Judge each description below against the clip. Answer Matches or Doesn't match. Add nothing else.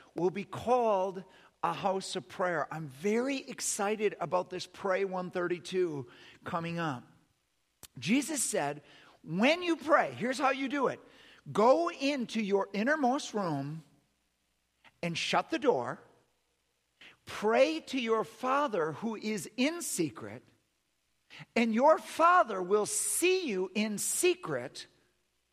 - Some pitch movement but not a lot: Doesn't match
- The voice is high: Matches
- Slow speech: Matches